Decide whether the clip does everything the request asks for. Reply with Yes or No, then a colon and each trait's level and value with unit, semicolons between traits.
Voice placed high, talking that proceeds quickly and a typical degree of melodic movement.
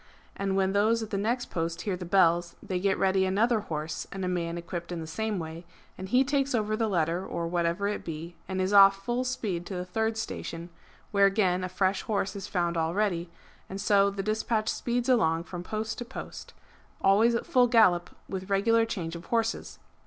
Yes: high, 195 Hz; fast, 210 wpm; average, 4.0 semitones